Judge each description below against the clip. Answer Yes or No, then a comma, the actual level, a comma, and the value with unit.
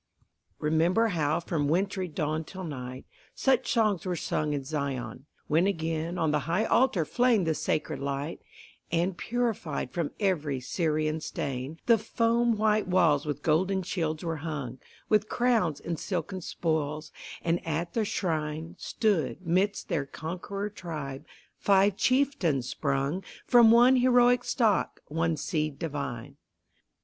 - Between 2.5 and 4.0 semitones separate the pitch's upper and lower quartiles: No, average, 5.1 semitones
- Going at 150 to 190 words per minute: No, average, 140 wpm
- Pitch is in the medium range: Yes, medium, 165 Hz